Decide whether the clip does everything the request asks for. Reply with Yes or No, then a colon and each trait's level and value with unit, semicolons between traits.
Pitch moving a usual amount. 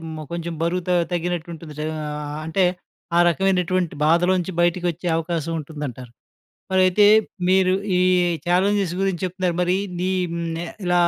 No: narrow, 1.8 semitones